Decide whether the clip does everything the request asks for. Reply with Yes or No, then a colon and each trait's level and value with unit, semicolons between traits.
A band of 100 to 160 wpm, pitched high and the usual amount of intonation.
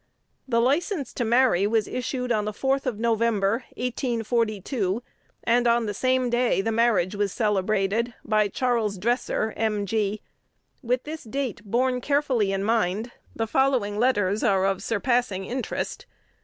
Yes: average, 140 wpm; high, 230 Hz; average, 3.3 semitones